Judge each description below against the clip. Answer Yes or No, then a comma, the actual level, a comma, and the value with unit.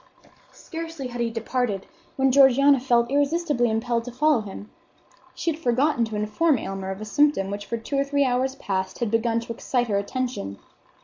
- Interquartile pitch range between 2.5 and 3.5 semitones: No, average, 4.1 semitones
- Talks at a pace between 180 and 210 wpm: Yes, average, 185 wpm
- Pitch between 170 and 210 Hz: No, high, 245 Hz